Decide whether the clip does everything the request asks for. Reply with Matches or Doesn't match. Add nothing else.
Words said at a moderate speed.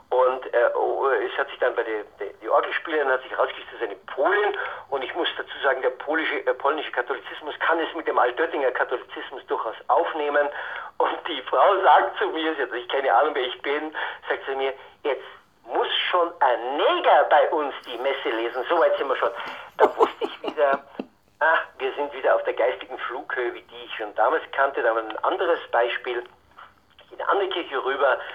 Doesn't match